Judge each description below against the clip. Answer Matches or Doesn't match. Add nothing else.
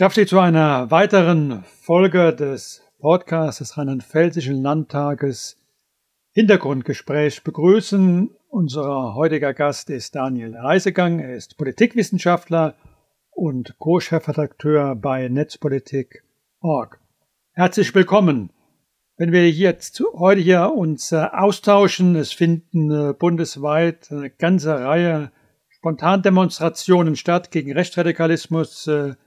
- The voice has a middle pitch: Matches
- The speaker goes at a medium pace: Doesn't match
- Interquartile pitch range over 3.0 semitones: Matches